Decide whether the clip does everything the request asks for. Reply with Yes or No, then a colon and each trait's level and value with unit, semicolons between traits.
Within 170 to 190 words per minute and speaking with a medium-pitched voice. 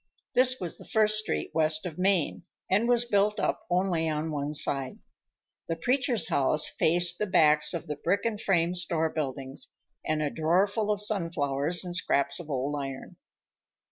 Yes: average, 175 wpm; medium, 170 Hz